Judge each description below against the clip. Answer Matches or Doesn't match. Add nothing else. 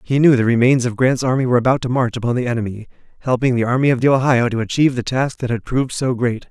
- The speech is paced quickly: Matches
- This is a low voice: Matches